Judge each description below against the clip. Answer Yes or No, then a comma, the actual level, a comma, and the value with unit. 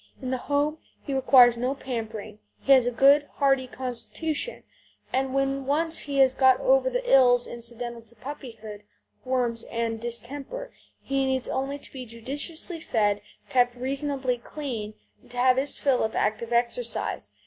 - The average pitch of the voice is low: No, very high, 260 Hz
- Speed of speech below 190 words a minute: Yes, average, 160 wpm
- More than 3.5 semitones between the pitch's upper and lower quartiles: No, average, 2.8 semitones